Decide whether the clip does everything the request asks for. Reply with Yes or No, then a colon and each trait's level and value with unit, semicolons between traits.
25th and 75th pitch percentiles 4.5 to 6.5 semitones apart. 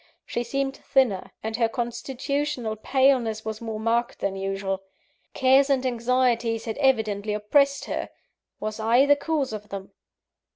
No: average, 3.6 semitones